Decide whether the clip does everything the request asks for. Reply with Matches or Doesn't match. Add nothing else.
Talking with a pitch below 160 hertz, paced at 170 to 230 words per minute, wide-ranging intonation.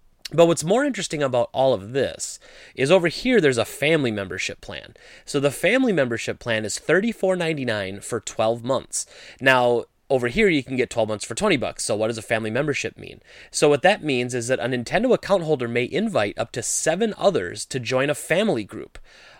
Matches